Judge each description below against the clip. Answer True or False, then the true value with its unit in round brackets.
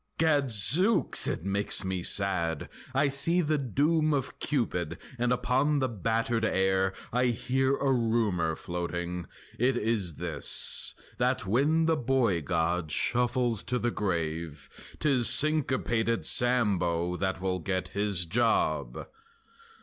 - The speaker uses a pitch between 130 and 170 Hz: False (115 Hz)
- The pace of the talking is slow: True (125 wpm)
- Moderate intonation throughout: False (6.2 semitones)